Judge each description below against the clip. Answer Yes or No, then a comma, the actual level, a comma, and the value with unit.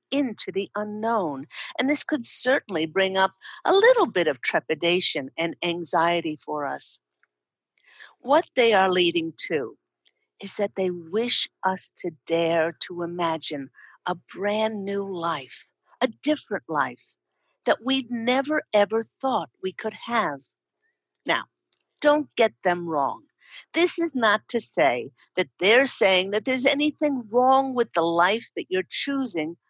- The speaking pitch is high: Yes, high, 205 Hz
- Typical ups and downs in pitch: No, wide, 7.5 semitones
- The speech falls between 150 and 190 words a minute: No, average, 140 wpm